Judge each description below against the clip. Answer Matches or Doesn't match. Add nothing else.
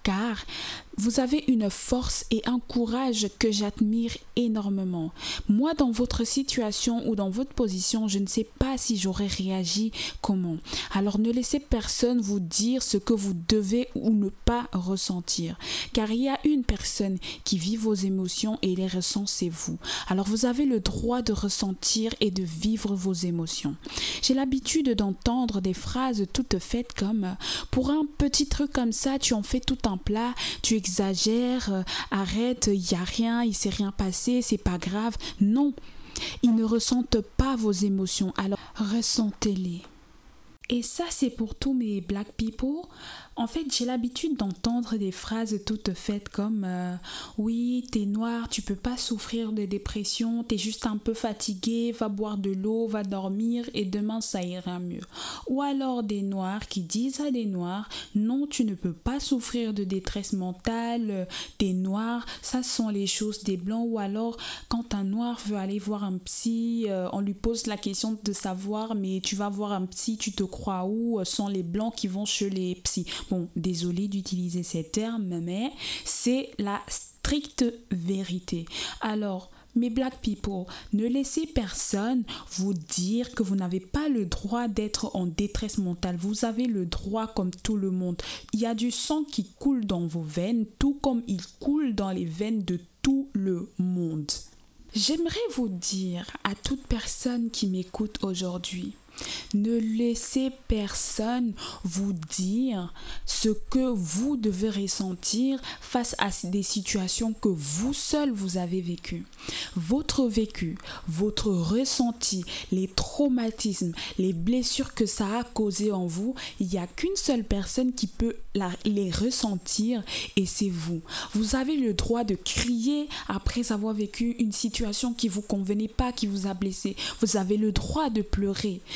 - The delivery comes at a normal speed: Matches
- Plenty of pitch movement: Doesn't match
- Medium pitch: Doesn't match